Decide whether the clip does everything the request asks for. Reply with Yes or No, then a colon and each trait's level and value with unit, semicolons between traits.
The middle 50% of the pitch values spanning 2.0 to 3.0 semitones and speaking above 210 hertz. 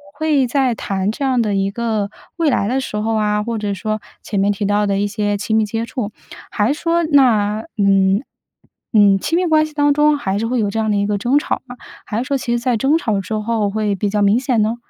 No: average, 4.1 semitones; high, 220 Hz